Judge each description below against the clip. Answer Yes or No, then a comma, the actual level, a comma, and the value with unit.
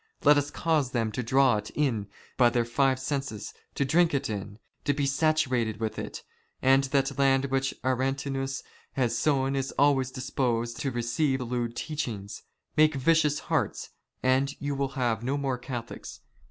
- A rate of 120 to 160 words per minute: No, average, 180 wpm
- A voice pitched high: No, low, 135 Hz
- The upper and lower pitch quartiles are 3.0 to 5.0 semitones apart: No, narrow, 2.6 semitones